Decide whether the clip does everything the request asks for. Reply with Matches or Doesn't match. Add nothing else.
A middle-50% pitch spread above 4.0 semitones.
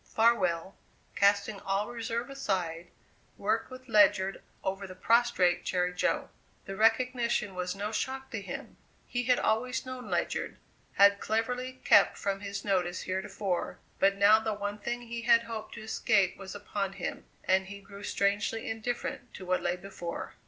Doesn't match